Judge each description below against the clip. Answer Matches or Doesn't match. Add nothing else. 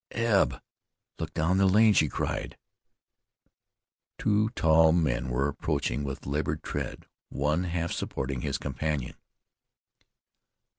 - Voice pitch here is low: Matches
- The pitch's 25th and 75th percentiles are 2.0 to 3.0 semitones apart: Doesn't match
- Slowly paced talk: Matches